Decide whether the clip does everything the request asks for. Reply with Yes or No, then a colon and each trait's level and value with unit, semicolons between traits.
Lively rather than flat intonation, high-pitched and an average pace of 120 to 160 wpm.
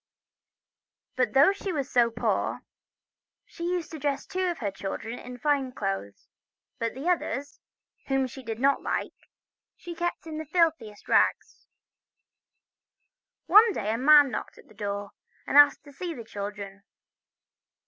Yes: wide, 6.3 semitones; very high, 270 Hz; average, 150 wpm